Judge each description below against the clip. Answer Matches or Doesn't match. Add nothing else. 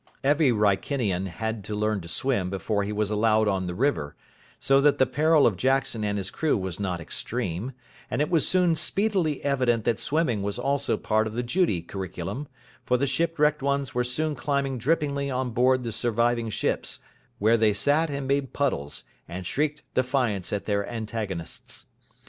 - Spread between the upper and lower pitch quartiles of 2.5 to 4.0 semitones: Doesn't match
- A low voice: Matches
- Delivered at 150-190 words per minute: Matches